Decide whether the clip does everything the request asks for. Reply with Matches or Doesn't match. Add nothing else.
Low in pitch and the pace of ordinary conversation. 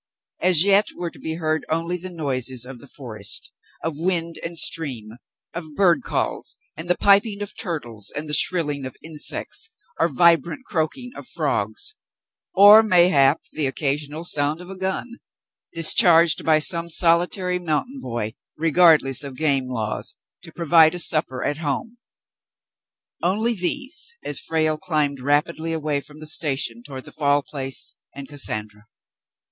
Doesn't match